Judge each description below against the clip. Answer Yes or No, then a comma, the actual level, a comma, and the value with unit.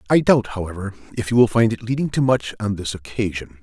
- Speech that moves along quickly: Yes, fast, 230 wpm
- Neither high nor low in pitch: No, low, 110 Hz